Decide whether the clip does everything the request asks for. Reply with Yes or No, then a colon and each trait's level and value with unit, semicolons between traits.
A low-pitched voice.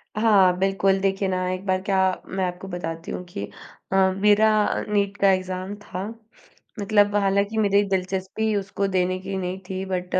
No: high, 195 Hz